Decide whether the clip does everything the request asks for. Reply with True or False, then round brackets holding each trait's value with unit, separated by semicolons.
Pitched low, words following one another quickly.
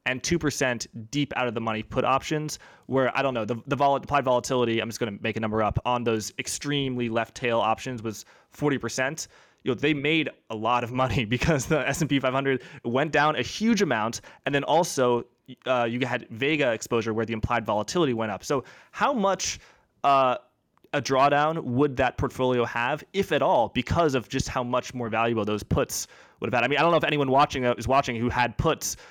True (130 Hz; 220 wpm)